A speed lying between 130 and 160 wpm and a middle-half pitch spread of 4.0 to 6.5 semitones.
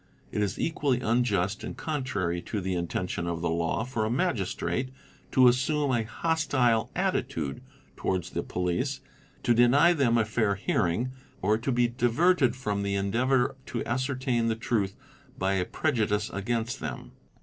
Yes: average, 155 wpm; average, 4.6 semitones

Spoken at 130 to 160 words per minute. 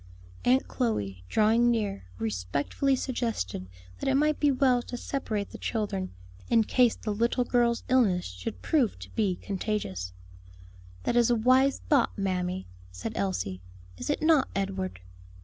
Yes: average, 150 wpm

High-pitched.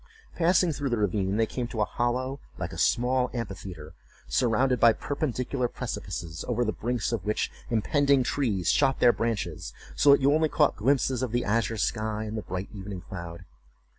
No: low, 120 Hz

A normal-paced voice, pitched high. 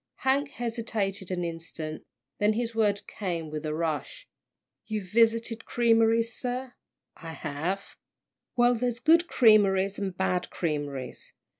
No: slow, 125 wpm; high, 205 Hz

